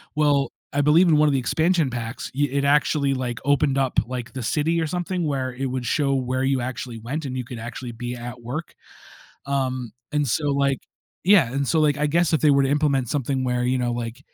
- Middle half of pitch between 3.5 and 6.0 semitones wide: No, average, 3.0 semitones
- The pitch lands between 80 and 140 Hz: Yes, low, 135 Hz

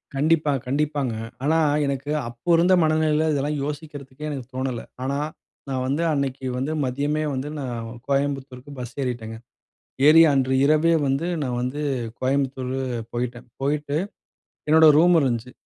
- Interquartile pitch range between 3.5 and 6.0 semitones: No, average, 2.7 semitones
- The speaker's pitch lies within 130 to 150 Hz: Yes, medium, 140 Hz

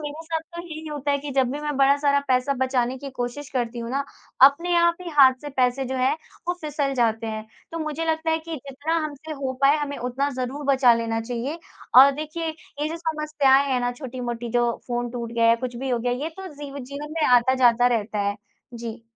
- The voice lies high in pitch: Yes, very high, 270 Hz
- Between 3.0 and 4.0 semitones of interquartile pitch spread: Yes, average, 3.5 semitones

